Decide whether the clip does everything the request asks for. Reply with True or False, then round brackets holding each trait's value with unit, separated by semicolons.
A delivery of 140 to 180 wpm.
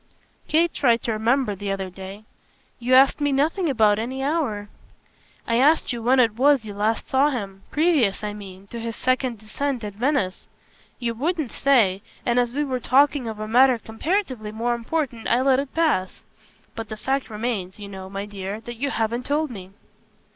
False (190 wpm)